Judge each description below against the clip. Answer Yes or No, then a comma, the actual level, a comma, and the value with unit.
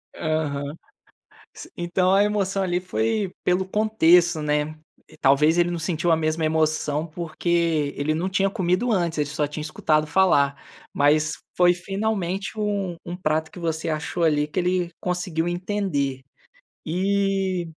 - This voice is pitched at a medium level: Yes, medium, 170 Hz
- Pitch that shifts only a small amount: No, average, 3.4 semitones